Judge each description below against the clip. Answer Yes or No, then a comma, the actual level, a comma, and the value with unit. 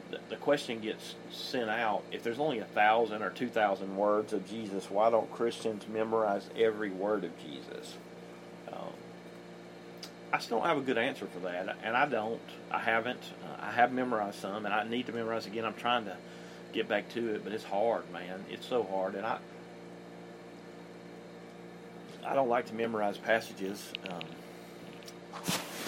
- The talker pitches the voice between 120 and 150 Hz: No, low, 110 Hz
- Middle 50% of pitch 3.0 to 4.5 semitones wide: No, narrow, 2.6 semitones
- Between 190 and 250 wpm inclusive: No, average, 165 wpm